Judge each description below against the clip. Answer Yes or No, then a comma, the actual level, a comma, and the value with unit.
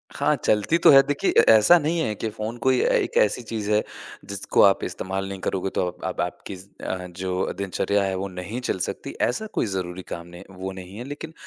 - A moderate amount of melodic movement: Yes, average, 3.6 semitones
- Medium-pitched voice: No, low, 100 Hz